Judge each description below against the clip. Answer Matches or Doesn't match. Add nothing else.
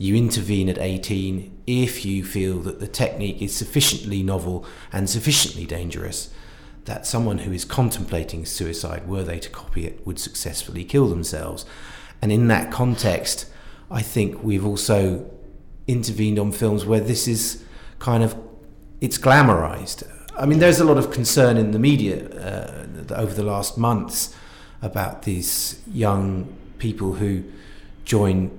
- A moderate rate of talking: Matches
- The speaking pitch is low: Matches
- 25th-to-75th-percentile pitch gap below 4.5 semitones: Matches